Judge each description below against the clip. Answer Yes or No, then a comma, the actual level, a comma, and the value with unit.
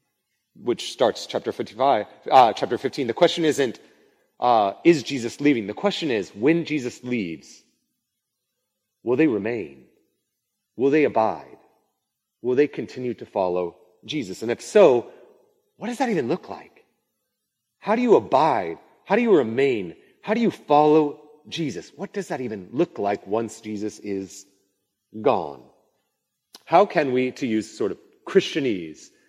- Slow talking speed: No, average, 150 wpm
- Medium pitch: Yes, medium, 150 Hz